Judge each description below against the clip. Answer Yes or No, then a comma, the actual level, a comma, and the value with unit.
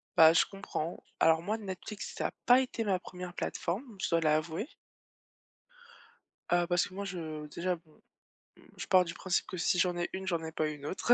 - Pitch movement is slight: No, average, 3.0 semitones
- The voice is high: No, medium, 175 Hz